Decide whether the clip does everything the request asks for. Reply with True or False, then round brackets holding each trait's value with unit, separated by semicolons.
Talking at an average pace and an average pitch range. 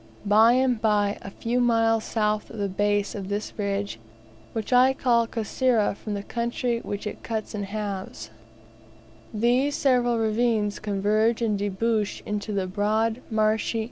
False (150 wpm; 2.3 semitones)